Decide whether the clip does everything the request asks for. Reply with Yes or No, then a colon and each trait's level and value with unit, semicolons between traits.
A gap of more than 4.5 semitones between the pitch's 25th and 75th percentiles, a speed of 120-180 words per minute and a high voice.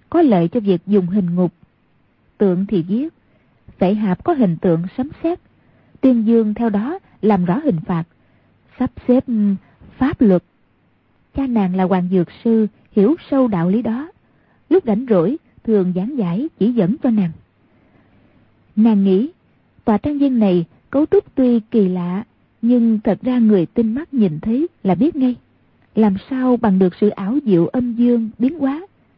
Yes: wide, 5.5 semitones; average, 170 wpm; high, 215 Hz